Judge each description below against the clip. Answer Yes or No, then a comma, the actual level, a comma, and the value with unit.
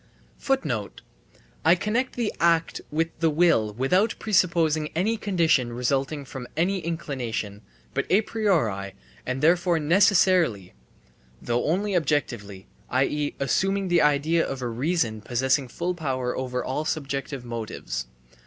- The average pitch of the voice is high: No, medium, 150 Hz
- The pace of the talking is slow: Yes, slow, 125 wpm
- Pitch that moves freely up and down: Yes, wide, 5.9 semitones